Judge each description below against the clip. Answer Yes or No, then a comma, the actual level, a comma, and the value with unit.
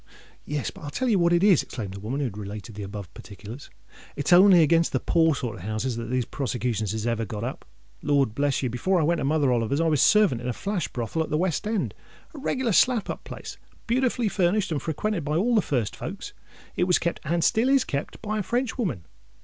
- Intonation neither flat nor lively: No, wide, 8.3 semitones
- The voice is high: No, medium, 150 Hz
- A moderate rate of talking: No, fast, 220 wpm